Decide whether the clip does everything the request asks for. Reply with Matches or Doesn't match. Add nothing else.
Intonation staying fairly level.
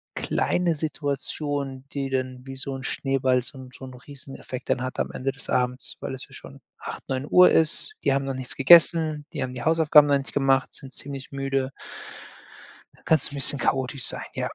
Matches